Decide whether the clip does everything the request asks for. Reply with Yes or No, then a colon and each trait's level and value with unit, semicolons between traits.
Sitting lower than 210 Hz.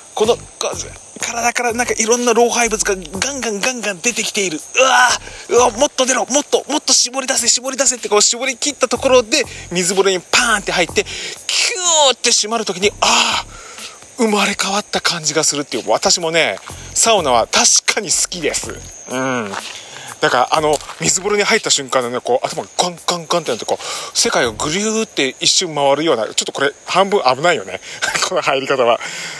No: high, 220 Hz